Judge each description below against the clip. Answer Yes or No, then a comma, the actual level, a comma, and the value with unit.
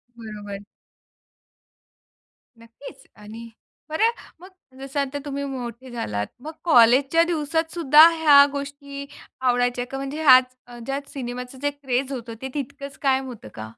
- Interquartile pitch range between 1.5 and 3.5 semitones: Yes, average, 2.7 semitones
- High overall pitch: Yes, very high, 270 Hz